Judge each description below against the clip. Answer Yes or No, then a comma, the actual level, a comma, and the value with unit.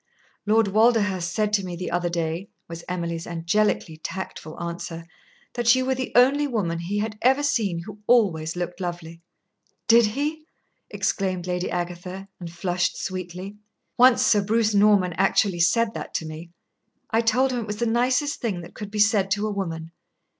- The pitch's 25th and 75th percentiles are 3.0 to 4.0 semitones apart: No, average, 4.6 semitones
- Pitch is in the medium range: No, high, 195 Hz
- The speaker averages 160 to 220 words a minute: Yes, average, 175 wpm